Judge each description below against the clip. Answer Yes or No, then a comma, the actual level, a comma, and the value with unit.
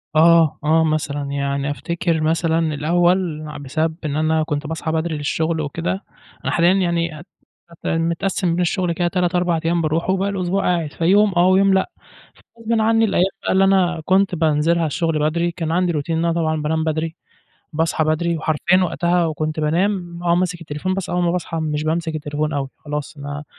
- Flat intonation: Yes, narrow, 2.3 semitones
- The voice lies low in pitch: No, medium, 165 Hz